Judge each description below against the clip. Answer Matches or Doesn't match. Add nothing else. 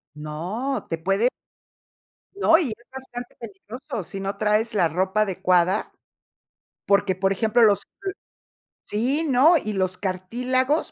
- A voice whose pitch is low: Doesn't match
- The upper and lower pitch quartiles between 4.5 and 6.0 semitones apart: Matches